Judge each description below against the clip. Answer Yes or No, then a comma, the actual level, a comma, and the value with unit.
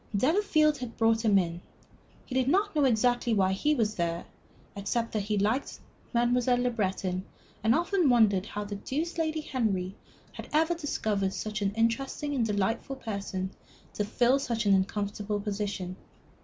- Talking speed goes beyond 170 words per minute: No, average, 160 wpm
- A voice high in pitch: Yes, high, 225 Hz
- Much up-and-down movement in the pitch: No, average, 4.8 semitones